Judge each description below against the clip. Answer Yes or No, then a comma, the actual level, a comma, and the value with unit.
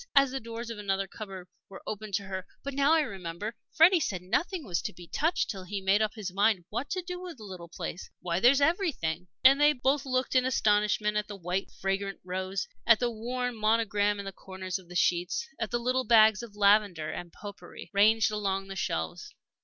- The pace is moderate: No, fast, 215 wpm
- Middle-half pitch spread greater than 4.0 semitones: Yes, average, 4.6 semitones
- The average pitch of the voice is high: Yes, high, 210 Hz